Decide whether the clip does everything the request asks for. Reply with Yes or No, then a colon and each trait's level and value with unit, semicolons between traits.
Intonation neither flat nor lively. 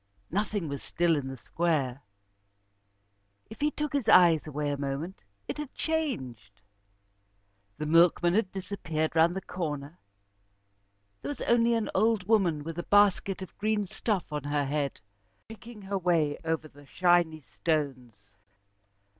No: wide, 5.8 semitones